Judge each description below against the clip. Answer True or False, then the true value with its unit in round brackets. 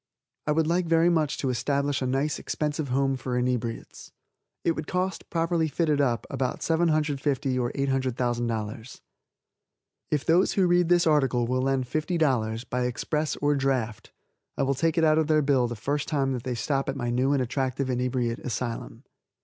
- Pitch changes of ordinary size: True (3.6 semitones)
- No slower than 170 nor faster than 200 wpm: True (175 wpm)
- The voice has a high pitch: False (135 Hz)